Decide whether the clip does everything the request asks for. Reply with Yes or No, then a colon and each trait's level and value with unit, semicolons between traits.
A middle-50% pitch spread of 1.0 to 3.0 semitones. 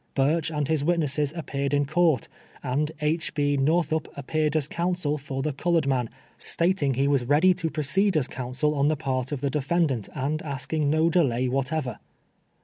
Yes: average, 2.7 semitones